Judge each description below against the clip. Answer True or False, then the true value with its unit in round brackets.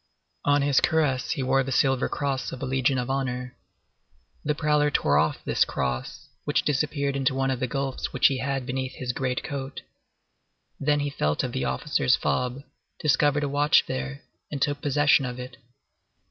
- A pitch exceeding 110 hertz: True (135 Hz)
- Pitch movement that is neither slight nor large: False (2.1 semitones)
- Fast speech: False (180 wpm)